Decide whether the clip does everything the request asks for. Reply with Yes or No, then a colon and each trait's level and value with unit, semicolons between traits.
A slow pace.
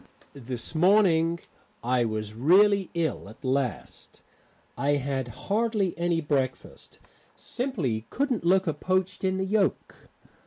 Yes: slow, 115 wpm